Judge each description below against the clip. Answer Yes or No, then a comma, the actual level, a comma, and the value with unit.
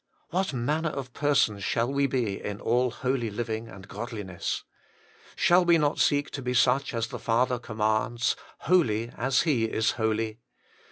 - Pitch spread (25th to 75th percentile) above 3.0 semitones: Yes, average, 3.9 semitones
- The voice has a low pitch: Yes, low, 120 Hz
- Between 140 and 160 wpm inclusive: No, average, 175 wpm